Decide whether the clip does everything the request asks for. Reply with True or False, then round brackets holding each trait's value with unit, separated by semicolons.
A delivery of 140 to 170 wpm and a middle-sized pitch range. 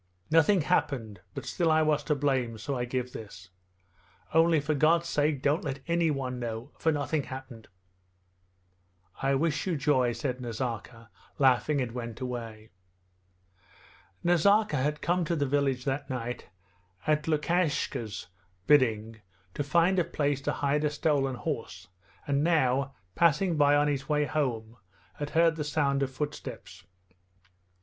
True (145 wpm; 3.6 semitones)